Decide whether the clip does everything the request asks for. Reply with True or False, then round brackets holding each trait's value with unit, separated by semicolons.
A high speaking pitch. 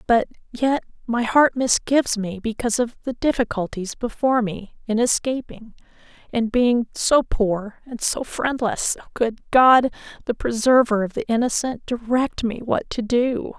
True (235 Hz)